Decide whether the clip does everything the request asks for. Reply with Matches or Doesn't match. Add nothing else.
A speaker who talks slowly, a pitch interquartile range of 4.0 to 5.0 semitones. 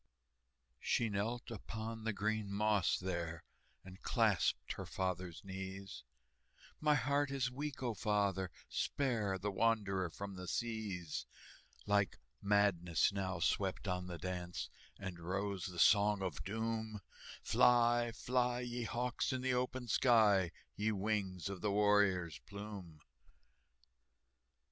Doesn't match